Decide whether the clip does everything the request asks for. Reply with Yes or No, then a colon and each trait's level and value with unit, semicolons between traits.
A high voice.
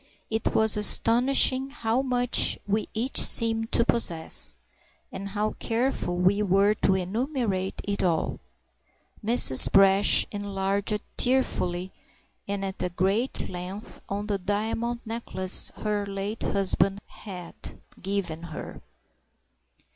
Yes: high, 205 Hz